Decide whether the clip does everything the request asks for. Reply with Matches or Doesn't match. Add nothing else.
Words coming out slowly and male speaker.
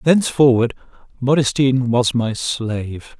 Matches